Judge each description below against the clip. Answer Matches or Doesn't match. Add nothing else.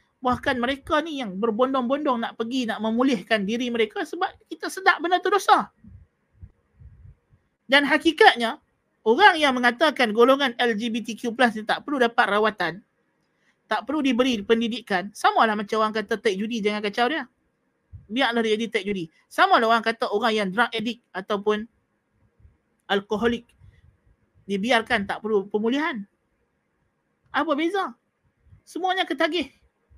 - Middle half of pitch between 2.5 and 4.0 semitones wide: Doesn't match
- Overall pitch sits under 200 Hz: Doesn't match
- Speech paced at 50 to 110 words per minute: Doesn't match